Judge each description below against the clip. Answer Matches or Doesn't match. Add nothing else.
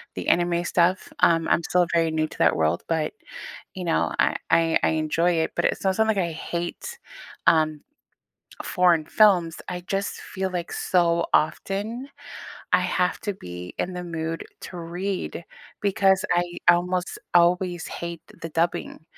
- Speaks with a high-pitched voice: Doesn't match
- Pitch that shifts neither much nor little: Doesn't match